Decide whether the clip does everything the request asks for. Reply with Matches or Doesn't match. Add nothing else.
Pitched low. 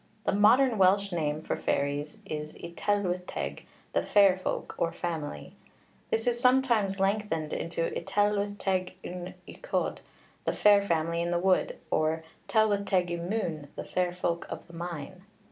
Doesn't match